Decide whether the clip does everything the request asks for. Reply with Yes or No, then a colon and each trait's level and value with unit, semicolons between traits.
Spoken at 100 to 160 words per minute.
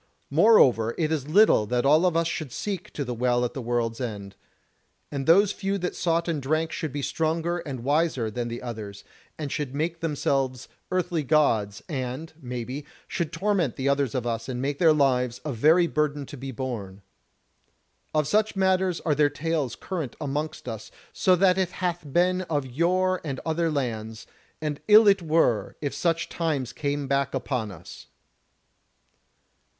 No: average, 175 wpm